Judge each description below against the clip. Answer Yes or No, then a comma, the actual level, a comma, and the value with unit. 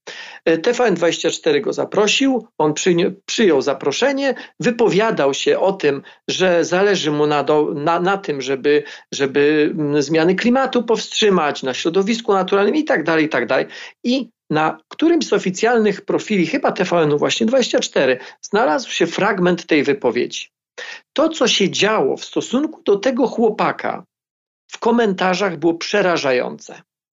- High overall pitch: Yes, high, 195 Hz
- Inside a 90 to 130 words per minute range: Yes, average, 120 wpm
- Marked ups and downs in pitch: Yes, wide, 7.0 semitones